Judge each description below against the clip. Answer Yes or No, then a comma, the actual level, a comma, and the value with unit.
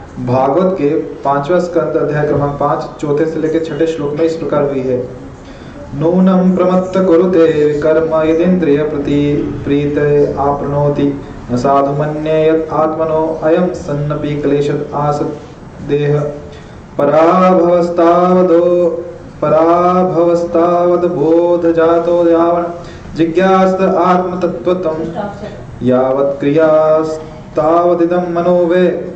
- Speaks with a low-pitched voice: No, medium, 160 Hz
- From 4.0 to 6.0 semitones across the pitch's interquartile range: No, average, 2.9 semitones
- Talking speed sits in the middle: No, slow, 35 wpm